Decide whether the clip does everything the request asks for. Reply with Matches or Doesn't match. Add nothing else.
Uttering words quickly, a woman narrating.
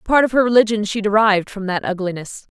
Matches